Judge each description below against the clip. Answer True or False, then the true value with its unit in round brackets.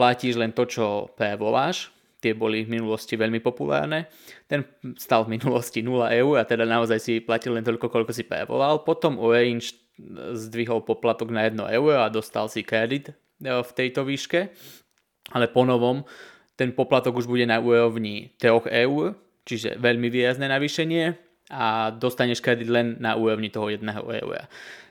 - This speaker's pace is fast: False (155 wpm)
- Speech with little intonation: True (2.1 semitones)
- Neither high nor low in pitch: False (120 Hz)